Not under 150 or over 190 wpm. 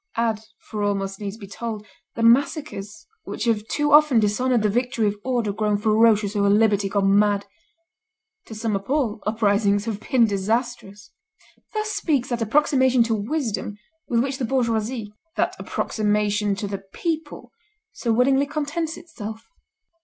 Yes: average, 155 wpm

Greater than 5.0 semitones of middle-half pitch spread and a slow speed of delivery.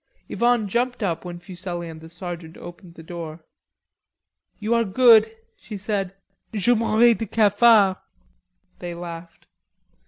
No: average, 4.5 semitones; slow, 130 wpm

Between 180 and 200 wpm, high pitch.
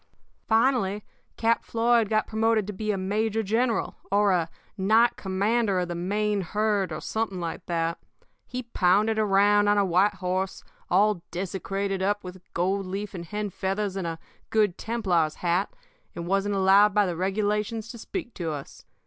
No: average, 165 wpm; high, 200 Hz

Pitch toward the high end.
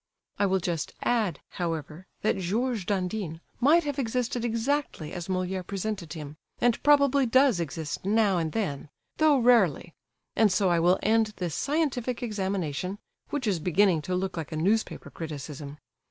Yes: high, 195 Hz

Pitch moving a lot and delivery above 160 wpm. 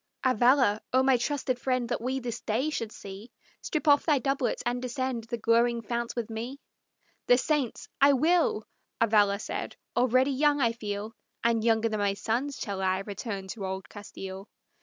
No: average, 3.6 semitones; average, 175 wpm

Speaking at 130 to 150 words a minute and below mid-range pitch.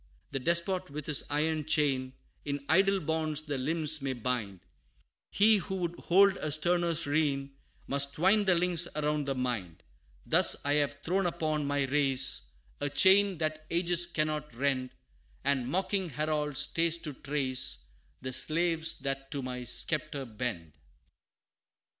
No: average, 145 wpm; medium, 150 Hz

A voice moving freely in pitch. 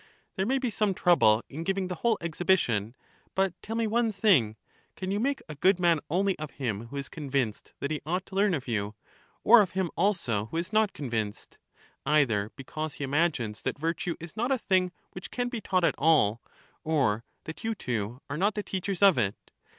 Yes: wide, 6.9 semitones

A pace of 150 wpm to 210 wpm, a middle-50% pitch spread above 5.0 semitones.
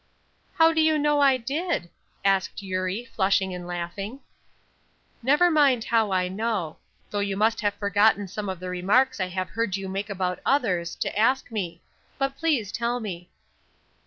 Yes: average, 165 wpm; wide, 5.5 semitones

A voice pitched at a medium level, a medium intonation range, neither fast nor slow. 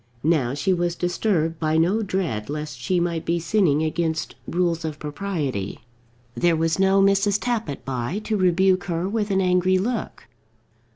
Yes: medium, 175 Hz; average, 3.5 semitones; average, 160 wpm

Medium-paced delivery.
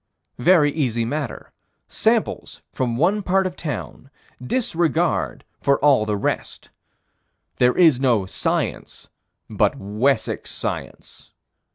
No: slow, 105 wpm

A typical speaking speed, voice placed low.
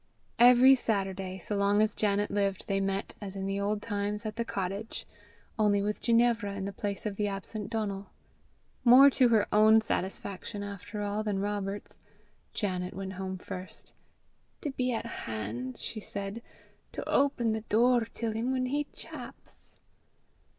No: average, 160 wpm; high, 205 Hz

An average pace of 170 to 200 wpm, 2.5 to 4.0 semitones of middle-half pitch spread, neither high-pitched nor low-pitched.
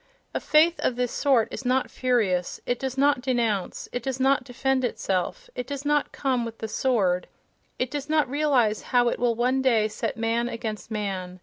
No: average, 195 wpm; average, 3.1 semitones; high, 245 Hz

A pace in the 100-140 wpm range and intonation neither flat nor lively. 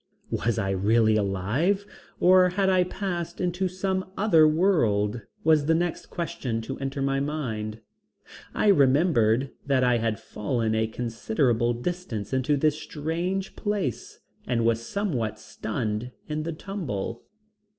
No: slow, 135 wpm; wide, 7.6 semitones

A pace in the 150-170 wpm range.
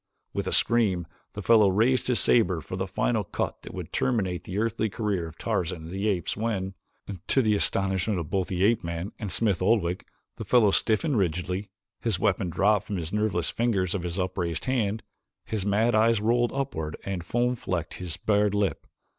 No: average, 190 wpm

